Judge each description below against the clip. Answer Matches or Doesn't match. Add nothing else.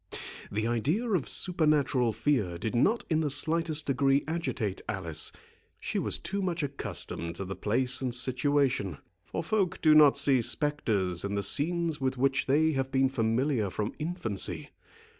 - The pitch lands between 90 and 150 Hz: Matches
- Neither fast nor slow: Matches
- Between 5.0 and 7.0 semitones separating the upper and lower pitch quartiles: Matches